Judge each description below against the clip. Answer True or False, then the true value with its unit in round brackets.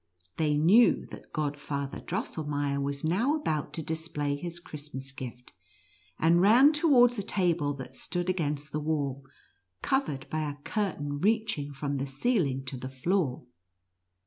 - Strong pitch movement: False (4.6 semitones)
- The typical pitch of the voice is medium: True (150 Hz)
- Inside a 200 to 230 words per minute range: False (145 wpm)